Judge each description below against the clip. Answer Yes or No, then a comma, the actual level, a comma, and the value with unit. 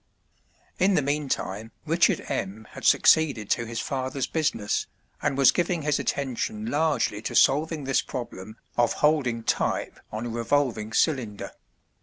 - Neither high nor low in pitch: No, low, 130 Hz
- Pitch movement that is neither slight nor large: Yes, average, 4.9 semitones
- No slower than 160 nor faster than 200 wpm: No, average, 140 wpm